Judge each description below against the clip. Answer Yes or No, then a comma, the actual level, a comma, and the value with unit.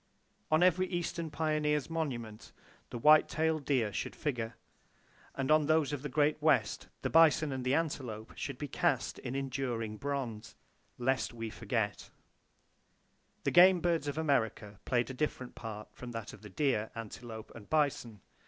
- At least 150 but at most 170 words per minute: Yes, average, 160 wpm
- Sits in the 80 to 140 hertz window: Yes, low, 135 Hz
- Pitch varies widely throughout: No, average, 5.0 semitones